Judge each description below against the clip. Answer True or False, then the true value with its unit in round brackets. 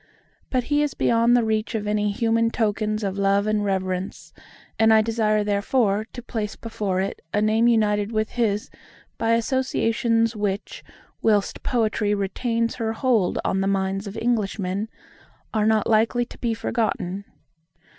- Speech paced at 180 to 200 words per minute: False (155 wpm)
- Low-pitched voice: False (215 Hz)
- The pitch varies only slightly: True (2.1 semitones)